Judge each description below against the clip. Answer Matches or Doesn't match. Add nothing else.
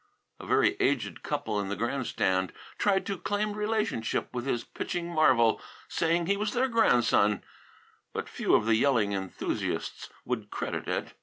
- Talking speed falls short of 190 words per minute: Matches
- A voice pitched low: Matches